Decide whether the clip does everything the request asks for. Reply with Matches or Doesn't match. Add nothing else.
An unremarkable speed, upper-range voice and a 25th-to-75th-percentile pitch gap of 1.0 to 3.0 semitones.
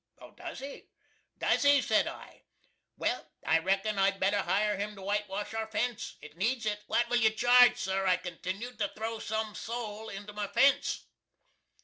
Matches